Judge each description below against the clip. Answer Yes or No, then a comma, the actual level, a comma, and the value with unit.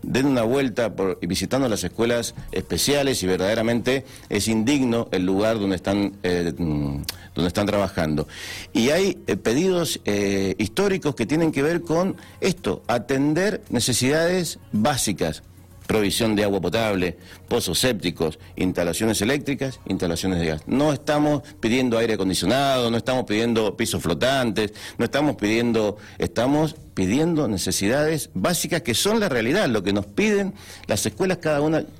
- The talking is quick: No, average, 140 wpm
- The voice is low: Yes, low, 110 Hz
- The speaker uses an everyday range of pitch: No, wide, 6.5 semitones